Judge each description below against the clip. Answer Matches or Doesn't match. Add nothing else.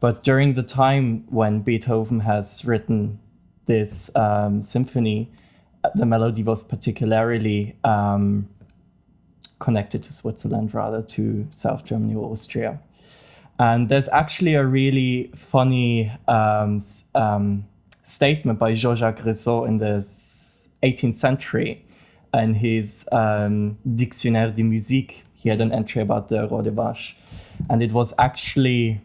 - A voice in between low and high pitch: Doesn't match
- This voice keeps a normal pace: Doesn't match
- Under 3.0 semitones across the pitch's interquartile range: Matches